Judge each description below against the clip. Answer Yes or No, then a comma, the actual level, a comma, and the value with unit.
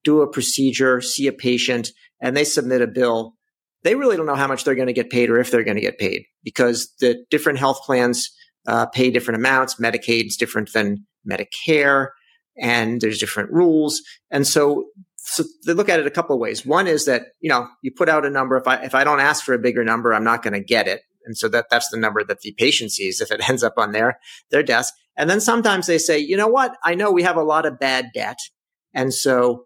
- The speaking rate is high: Yes, fast, 245 wpm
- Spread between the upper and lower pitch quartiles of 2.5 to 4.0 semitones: No, average, 4.5 semitones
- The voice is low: Yes, low, 130 Hz